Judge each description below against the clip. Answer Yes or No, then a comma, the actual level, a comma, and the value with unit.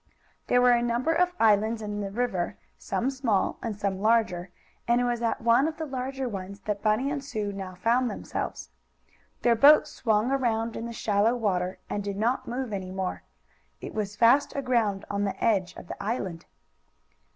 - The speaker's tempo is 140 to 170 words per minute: No, average, 185 wpm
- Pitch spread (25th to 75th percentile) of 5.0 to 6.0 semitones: No, average, 3.5 semitones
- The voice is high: Yes, high, 225 Hz